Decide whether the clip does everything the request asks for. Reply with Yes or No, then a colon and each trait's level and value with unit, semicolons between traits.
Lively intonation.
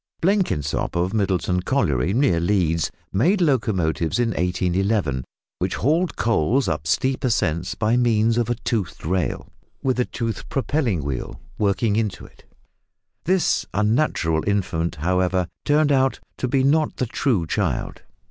Yes: wide, 6.8 semitones